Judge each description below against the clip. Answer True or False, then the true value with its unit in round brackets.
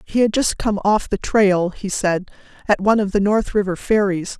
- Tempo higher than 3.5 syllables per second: True (4.9 syllables/s)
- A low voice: False (200 Hz)